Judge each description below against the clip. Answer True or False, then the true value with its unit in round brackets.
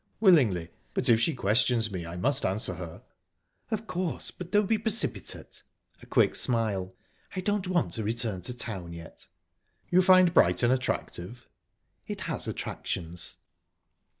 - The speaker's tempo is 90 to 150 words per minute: True (145 wpm)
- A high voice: False (120 Hz)